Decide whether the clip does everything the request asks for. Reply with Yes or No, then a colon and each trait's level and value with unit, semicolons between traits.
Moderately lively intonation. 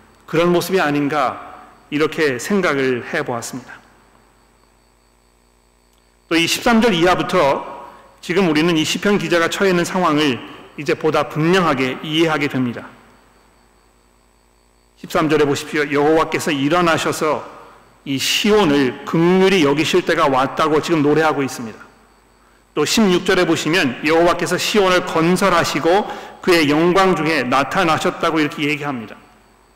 Yes: average, 4.8 semitones